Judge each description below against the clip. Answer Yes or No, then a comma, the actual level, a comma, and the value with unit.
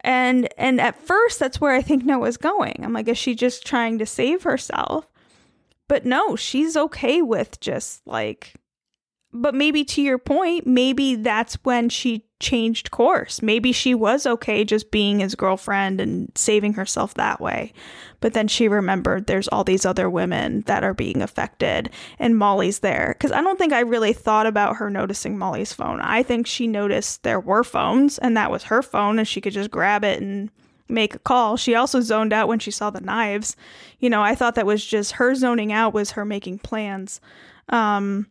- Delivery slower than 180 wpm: No, average, 195 wpm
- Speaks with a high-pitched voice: Yes, high, 230 Hz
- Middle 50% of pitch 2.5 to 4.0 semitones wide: Yes, average, 3.5 semitones